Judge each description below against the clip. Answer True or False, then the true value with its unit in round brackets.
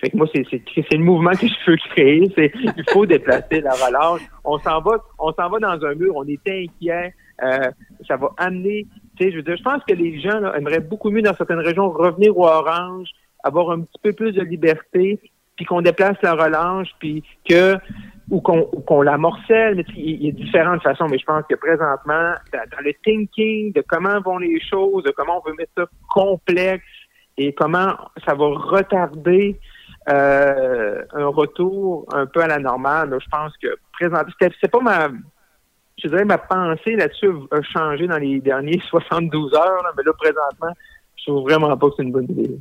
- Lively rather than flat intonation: False (4.1 semitones)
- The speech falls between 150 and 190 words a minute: False (205 wpm)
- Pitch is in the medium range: True (175 Hz)